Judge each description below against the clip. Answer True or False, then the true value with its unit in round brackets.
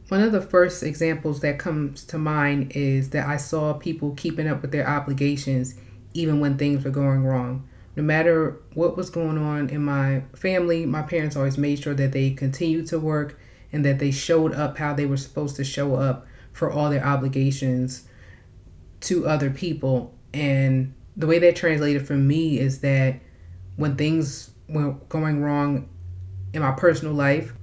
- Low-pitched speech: False (145 Hz)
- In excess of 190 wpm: False (175 wpm)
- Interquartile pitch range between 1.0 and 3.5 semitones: True (2.5 semitones)